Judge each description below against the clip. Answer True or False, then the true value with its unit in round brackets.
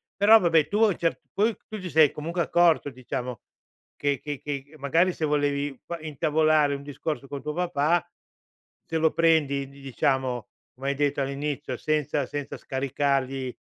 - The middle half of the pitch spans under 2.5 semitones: False (2.8 semitones)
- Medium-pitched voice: True (145 Hz)